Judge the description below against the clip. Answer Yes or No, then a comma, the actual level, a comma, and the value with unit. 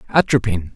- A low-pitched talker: Yes, low, 105 Hz